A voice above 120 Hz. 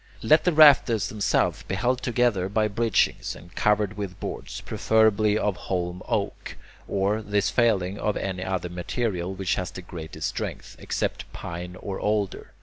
No: low, 100 Hz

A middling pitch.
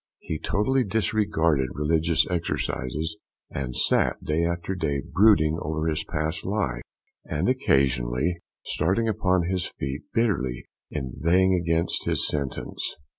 No: very low, 80 Hz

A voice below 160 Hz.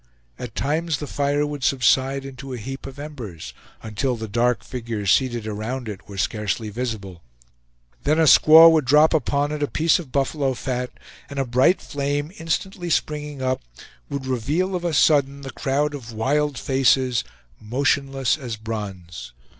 Yes: low, 135 Hz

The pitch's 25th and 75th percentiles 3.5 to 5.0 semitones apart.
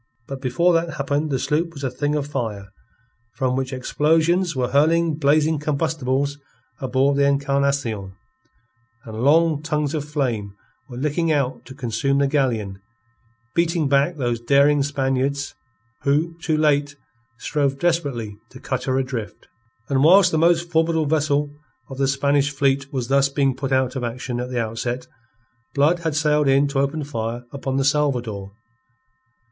No: average, 2.7 semitones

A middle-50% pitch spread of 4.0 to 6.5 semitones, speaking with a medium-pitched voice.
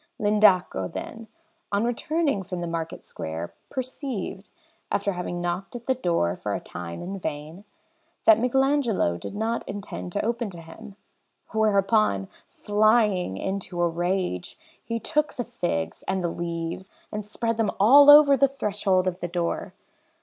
No: average, 4.9 semitones; high, 200 Hz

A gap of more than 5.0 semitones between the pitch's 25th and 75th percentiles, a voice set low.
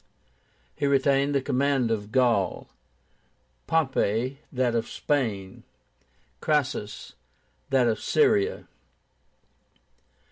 No: average, 3.8 semitones; low, 130 Hz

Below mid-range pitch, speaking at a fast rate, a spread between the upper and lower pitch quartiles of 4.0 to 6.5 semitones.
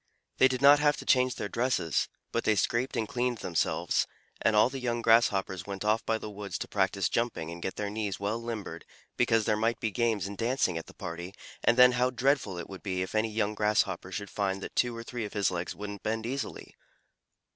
No: low, 110 Hz; fast, 225 wpm; average, 3.3 semitones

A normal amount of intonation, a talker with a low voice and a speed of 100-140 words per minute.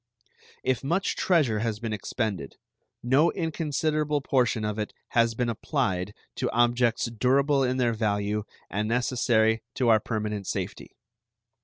Yes: average, 3.9 semitones; low, 120 Hz; slow, 135 wpm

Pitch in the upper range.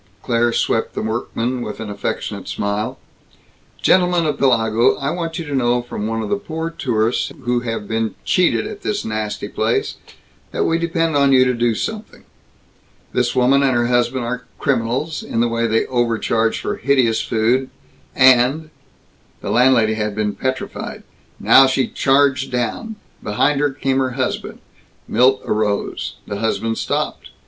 No: low, 125 Hz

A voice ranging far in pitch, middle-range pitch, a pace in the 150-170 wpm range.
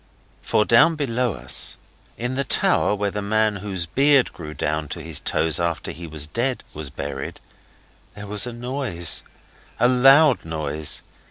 No: wide, 7.4 semitones; low, 105 Hz; average, 160 wpm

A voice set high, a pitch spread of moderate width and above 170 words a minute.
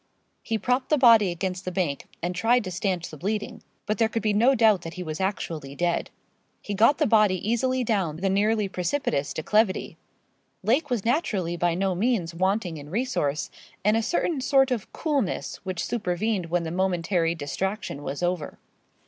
Yes: high, 195 Hz; average, 4.6 semitones; average, 180 wpm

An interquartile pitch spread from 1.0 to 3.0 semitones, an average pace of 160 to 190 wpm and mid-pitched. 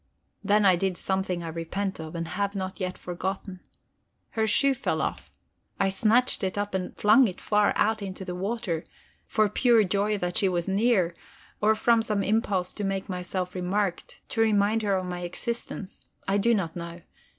No: average, 2.7 semitones; average, 185 wpm; high, 195 Hz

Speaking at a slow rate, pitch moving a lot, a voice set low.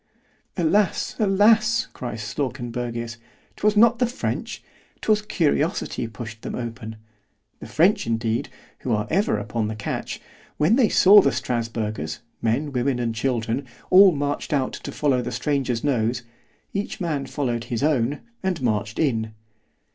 Yes: slow, 130 wpm; wide, 6.5 semitones; low, 125 Hz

